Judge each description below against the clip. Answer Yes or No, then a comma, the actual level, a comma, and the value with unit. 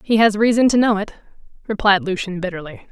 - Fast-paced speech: No, average, 185 wpm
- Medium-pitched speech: No, high, 205 Hz